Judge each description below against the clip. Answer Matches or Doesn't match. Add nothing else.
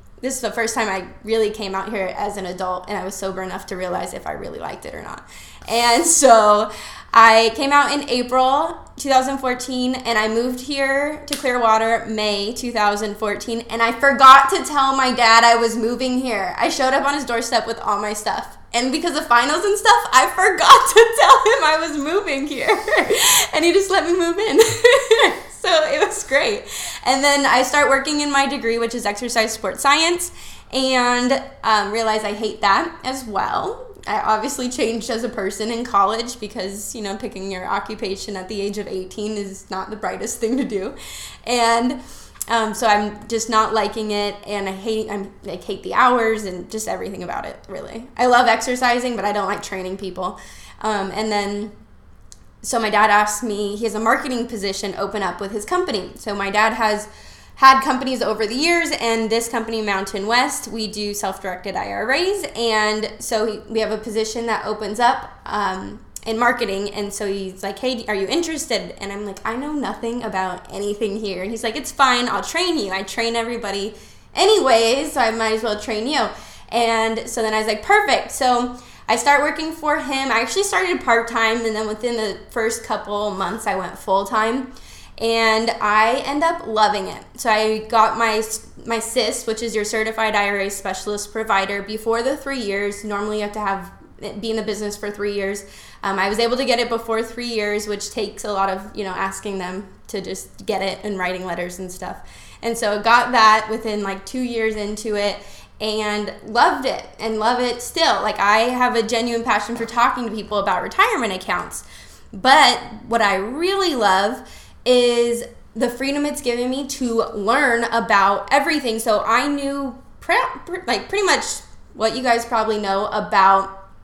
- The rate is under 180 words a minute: Doesn't match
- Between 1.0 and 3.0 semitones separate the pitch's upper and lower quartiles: Doesn't match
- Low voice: Doesn't match